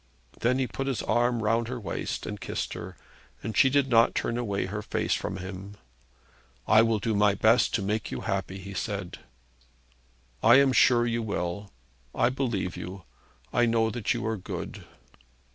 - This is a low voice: Yes, low, 110 Hz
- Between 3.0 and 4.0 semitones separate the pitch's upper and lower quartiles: Yes, average, 3.3 semitones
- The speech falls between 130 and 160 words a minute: No, average, 180 wpm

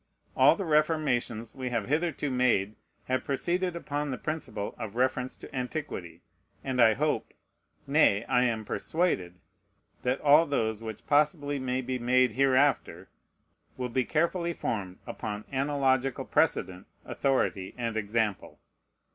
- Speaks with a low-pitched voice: Yes, low, 130 Hz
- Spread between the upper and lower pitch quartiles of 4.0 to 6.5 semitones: Yes, average, 4.6 semitones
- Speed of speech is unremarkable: No, slow, 130 wpm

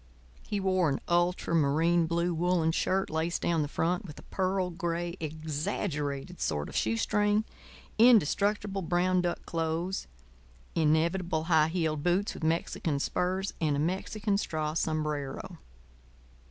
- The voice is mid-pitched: Yes, medium, 170 Hz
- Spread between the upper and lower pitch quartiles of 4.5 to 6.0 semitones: No, average, 2.9 semitones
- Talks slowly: Yes, slow, 125 wpm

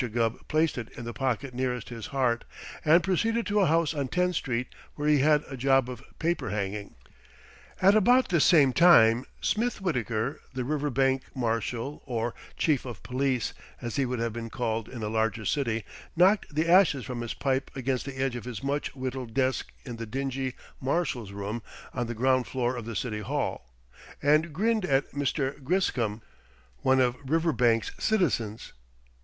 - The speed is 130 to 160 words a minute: No, average, 175 wpm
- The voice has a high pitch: No, low, 130 Hz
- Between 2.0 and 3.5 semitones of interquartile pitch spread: No, average, 4.2 semitones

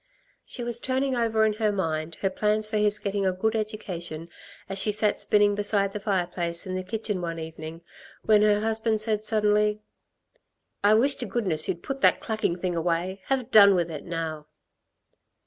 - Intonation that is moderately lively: Yes, average, 3.7 semitones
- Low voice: No, high, 205 Hz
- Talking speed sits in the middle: Yes, average, 180 wpm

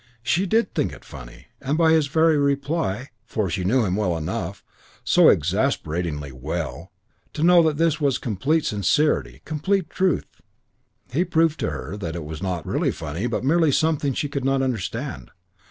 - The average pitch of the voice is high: No, low, 135 Hz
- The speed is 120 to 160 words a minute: No, average, 170 wpm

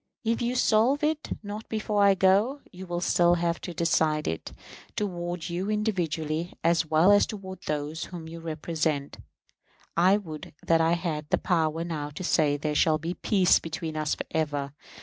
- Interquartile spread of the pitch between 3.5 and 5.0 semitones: Yes, average, 3.8 semitones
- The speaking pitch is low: No, medium, 170 Hz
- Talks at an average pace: Yes, average, 175 wpm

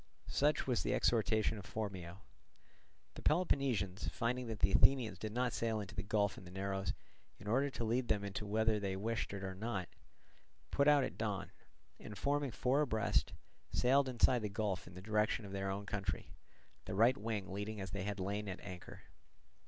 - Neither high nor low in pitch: No, low, 105 Hz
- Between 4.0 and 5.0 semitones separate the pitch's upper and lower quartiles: No, average, 3.3 semitones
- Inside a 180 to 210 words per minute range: Yes, average, 190 wpm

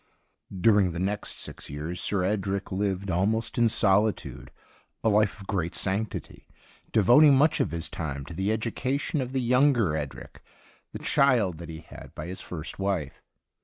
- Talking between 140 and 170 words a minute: Yes, average, 165 wpm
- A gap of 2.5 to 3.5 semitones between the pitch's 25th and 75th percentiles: No, average, 4.3 semitones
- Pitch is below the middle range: Yes, low, 100 Hz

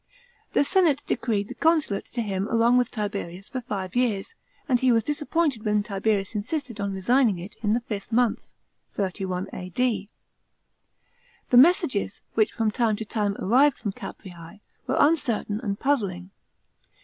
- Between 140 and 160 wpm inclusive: Yes, average, 150 wpm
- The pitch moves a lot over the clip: No, average, 4.1 semitones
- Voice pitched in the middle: No, high, 215 Hz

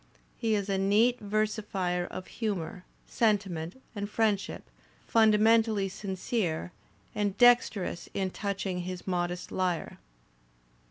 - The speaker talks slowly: Yes, slow, 110 wpm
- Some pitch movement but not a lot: Yes, average, 3.0 semitones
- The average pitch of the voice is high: Yes, high, 200 Hz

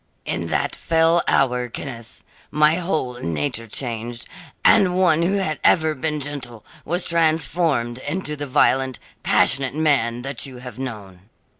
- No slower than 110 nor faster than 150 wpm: Yes, average, 140 wpm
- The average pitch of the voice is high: No, low, 135 Hz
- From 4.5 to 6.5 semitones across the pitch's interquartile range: Yes, average, 4.8 semitones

